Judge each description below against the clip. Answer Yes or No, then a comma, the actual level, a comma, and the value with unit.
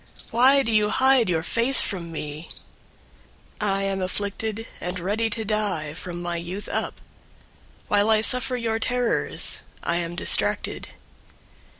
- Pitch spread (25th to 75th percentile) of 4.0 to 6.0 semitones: Yes, average, 4.6 semitones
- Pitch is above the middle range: Yes, high, 205 Hz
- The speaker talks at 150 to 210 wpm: No, average, 140 wpm